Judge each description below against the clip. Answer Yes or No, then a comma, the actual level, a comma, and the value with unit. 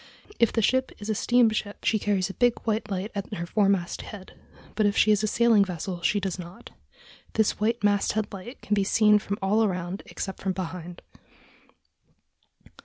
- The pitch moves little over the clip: Yes, narrow, 2.3 semitones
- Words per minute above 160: Yes, average, 180 wpm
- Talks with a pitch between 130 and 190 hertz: No, high, 205 Hz